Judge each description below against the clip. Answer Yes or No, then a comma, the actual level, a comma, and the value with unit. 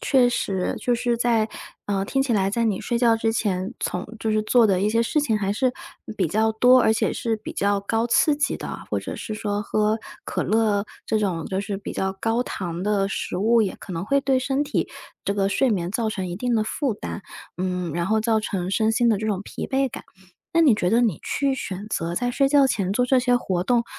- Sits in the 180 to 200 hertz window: No, high, 220 Hz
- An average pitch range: Yes, average, 3.7 semitones